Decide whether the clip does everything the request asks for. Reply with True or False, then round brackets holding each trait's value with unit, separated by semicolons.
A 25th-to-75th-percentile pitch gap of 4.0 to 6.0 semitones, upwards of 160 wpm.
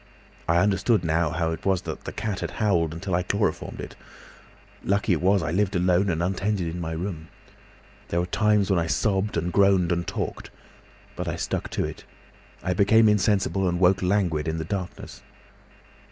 False (2.8 semitones; 180 wpm)